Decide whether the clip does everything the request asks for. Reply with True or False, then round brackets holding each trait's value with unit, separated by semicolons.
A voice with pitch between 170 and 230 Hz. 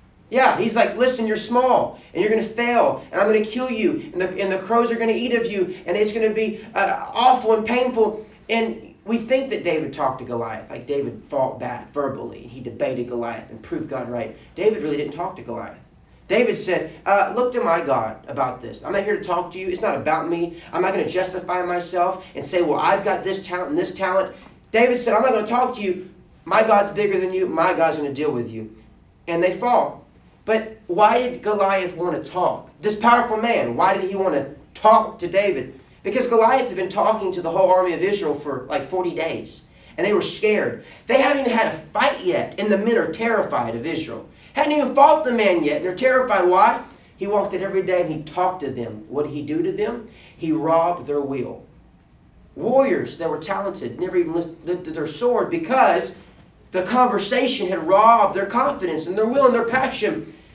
True (190 Hz)